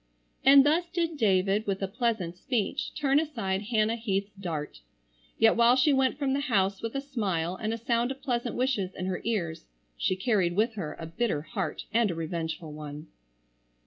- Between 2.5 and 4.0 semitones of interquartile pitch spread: No, average, 5.3 semitones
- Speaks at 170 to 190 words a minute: Yes, average, 185 wpm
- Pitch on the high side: Yes, high, 215 Hz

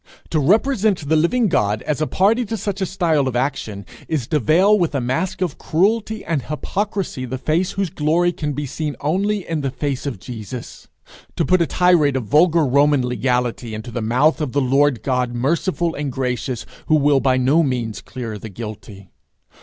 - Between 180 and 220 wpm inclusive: Yes, average, 195 wpm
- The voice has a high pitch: No, medium, 145 Hz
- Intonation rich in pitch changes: Yes, wide, 5.8 semitones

